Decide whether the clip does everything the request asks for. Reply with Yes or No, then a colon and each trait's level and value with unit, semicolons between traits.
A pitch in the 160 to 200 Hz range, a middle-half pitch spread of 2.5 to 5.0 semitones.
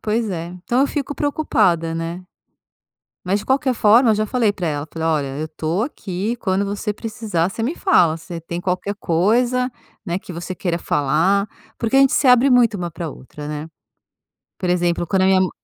No: high, 190 Hz; wide, 5.5 semitones